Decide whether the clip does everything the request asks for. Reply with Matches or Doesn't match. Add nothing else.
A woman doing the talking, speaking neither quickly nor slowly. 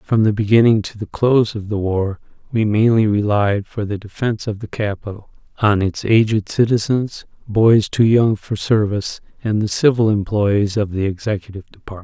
Doesn't match